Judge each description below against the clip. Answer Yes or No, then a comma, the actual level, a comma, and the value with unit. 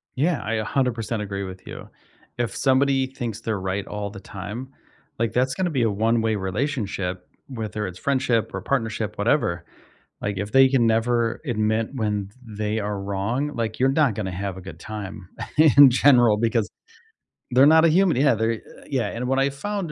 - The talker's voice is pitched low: Yes, low, 115 Hz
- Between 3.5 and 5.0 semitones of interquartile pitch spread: Yes, average, 4.4 semitones